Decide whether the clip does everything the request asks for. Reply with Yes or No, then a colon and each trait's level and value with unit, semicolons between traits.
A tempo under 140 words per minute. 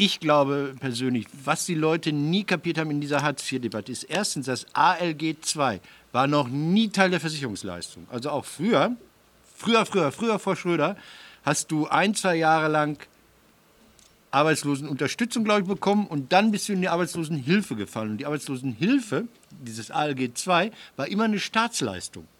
No: average, 160 wpm